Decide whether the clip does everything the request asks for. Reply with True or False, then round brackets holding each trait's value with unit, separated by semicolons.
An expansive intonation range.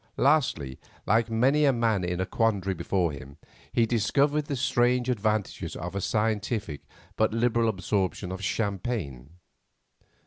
False (4.6 semitones)